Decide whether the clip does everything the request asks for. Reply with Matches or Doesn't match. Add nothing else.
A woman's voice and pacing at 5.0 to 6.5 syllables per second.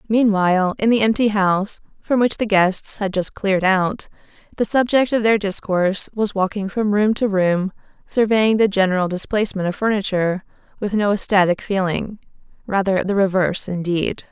Matches